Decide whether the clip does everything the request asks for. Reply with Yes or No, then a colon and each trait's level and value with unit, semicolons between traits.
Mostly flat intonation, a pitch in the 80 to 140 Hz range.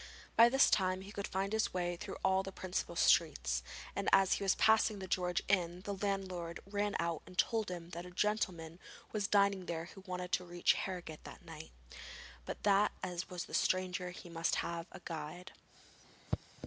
No: narrow, 2.3 semitones; medium, 185 Hz